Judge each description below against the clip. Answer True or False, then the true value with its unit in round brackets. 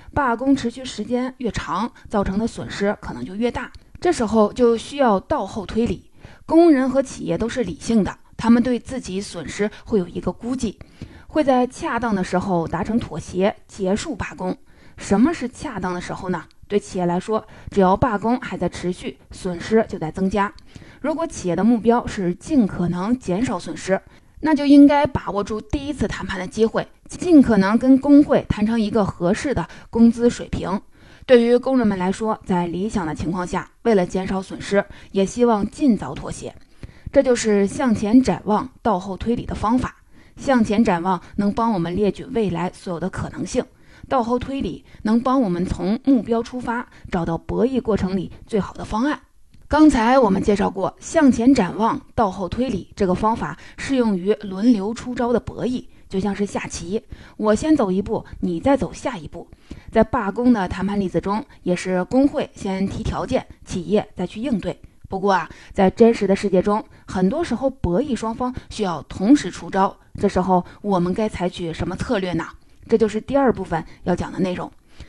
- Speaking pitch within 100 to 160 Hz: False (215 Hz)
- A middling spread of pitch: True (4.6 semitones)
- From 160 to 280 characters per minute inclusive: True (275 characters per minute)